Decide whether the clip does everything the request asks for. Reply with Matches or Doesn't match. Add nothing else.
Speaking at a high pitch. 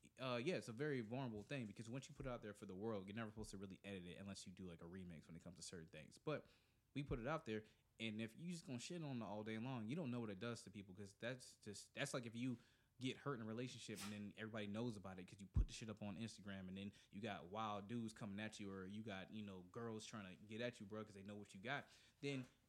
Doesn't match